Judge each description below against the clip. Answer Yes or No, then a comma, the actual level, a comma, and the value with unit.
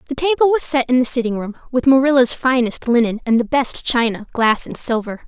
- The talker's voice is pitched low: No, very high, 250 Hz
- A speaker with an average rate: No, fast, 215 wpm